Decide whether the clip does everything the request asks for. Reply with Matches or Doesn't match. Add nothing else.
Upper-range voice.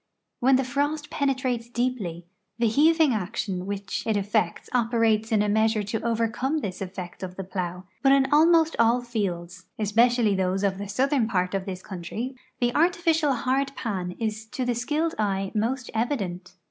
Matches